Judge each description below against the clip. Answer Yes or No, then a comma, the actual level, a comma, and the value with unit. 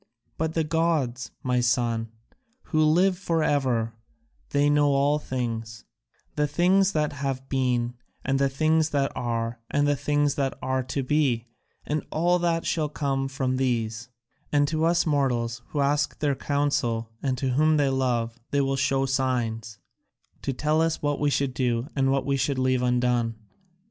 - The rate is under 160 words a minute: No, average, 165 wpm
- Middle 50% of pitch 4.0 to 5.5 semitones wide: No, average, 3.1 semitones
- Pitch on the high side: No, low, 135 Hz